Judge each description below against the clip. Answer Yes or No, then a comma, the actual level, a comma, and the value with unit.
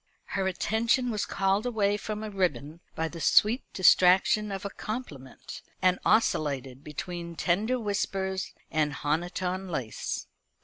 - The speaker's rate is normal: No, slow, 130 wpm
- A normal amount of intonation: Yes, average, 4.6 semitones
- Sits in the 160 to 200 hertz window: Yes, high, 190 Hz